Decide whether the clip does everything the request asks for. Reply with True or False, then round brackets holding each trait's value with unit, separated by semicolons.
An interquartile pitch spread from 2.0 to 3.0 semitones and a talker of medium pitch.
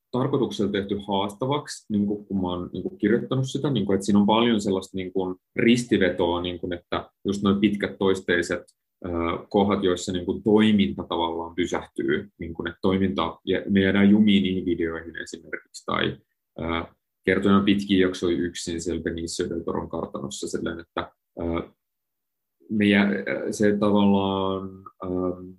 False (2.6 semitones; 95 Hz)